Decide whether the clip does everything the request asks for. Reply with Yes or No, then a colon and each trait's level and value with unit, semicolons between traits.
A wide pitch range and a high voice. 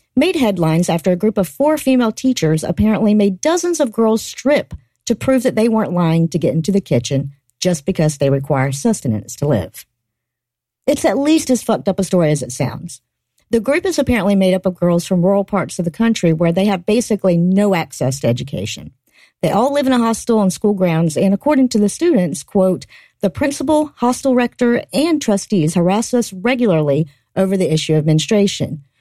Yes: wide, 6.7 semitones; high, 195 Hz